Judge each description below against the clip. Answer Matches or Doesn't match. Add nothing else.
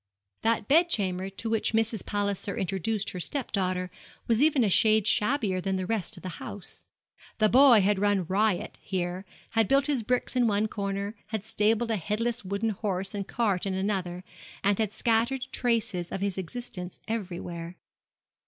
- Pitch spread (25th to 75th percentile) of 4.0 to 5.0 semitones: Doesn't match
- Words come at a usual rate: Matches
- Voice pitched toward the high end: Matches